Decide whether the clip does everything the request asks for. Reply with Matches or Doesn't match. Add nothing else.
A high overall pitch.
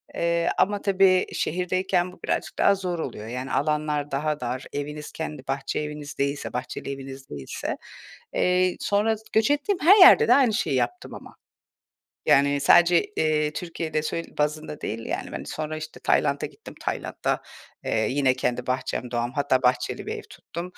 Doesn't match